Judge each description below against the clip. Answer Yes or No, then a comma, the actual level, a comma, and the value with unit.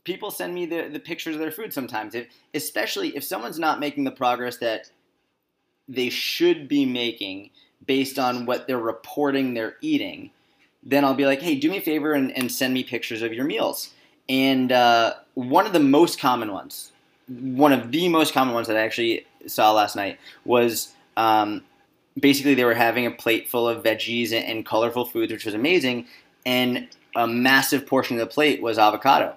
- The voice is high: No, low, 130 Hz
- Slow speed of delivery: No, average, 190 wpm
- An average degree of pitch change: Yes, average, 4.3 semitones